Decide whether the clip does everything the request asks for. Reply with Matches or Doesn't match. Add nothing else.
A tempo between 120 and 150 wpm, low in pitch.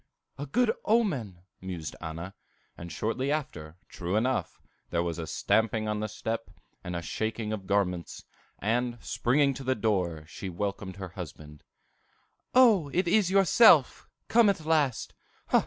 Matches